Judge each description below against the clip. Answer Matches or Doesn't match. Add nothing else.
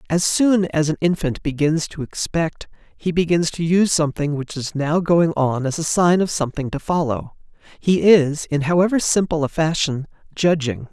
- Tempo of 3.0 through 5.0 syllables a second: Matches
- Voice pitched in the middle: Matches